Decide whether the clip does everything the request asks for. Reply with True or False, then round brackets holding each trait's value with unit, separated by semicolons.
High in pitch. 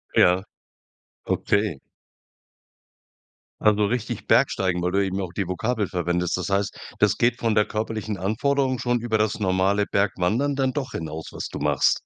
False (105 Hz)